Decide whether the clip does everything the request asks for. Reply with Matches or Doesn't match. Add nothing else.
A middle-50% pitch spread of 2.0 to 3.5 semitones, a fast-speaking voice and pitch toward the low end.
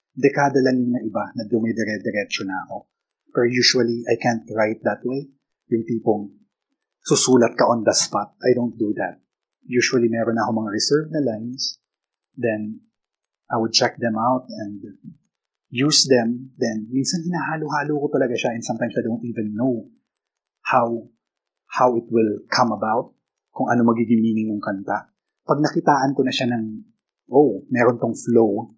Matches